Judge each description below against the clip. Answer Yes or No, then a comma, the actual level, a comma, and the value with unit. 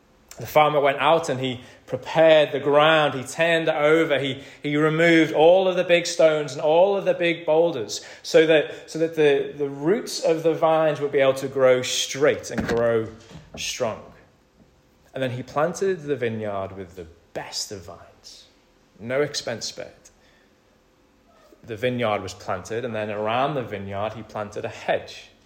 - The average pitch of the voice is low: No, medium, 145 Hz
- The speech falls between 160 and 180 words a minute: Yes, average, 170 wpm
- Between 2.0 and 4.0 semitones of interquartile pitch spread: No, average, 4.6 semitones